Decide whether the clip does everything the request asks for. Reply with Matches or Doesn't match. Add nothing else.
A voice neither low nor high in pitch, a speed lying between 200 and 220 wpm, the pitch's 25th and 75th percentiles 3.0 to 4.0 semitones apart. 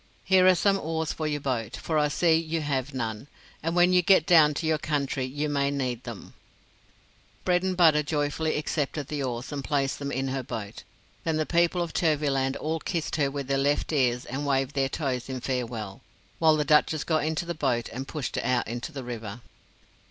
Matches